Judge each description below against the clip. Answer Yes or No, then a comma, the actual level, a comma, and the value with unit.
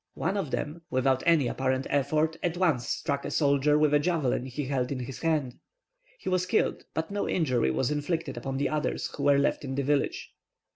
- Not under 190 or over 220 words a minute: Yes, fast, 205 wpm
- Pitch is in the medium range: Yes, medium, 145 Hz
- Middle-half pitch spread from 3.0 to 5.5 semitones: Yes, average, 3.3 semitones